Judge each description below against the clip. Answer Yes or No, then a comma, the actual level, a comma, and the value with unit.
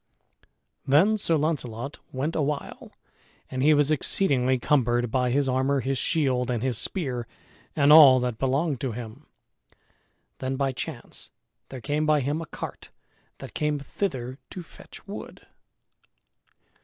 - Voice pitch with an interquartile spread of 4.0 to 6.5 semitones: No, average, 3.0 semitones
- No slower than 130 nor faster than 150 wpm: Yes, average, 140 wpm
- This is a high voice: No, low, 135 Hz